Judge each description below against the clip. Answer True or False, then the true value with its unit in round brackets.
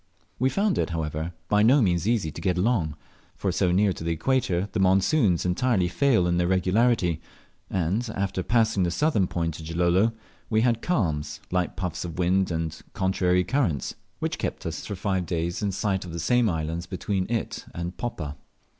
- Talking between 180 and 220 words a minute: True (185 wpm)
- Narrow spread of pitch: False (4.2 semitones)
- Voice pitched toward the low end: True (90 Hz)